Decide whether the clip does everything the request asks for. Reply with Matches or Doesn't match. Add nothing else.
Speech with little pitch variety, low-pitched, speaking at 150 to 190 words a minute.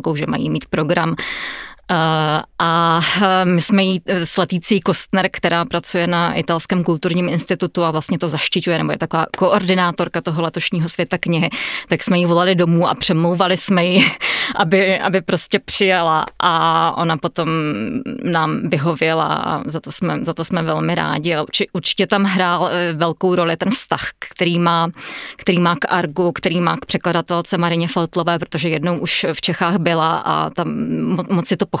Doesn't match